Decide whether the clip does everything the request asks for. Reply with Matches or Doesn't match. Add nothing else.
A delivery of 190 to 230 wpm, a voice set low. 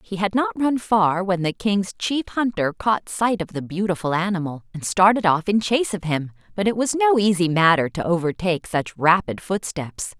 Doesn't match